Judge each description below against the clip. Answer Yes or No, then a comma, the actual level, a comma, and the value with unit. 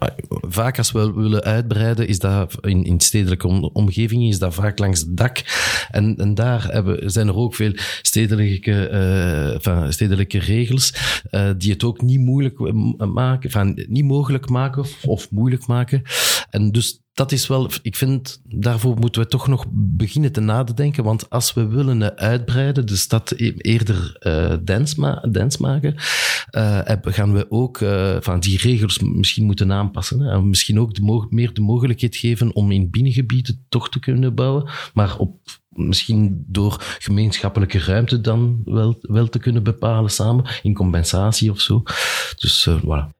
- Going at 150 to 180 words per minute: Yes, average, 165 wpm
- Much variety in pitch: No, average, 3.6 semitones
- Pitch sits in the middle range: No, low, 110 Hz